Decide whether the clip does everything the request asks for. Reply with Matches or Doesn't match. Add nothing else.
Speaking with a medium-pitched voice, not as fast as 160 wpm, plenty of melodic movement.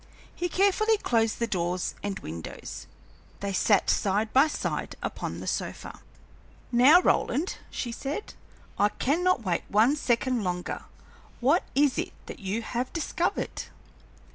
Doesn't match